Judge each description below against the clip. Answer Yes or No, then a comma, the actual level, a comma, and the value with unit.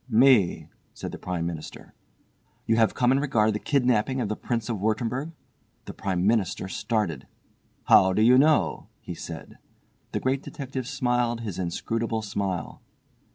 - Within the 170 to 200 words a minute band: No, average, 155 wpm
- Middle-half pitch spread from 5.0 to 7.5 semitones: No, average, 4.2 semitones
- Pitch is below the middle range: Yes, low, 115 Hz